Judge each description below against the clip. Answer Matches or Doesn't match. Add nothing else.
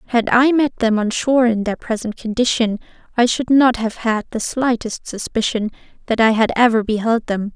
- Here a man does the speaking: Doesn't match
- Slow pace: Doesn't match